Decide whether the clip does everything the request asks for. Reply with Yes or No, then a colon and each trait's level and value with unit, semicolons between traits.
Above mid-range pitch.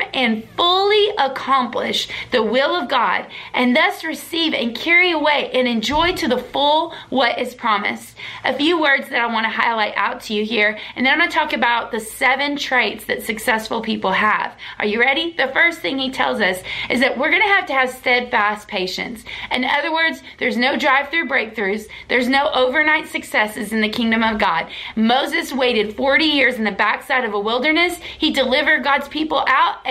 Yes: very high, 265 Hz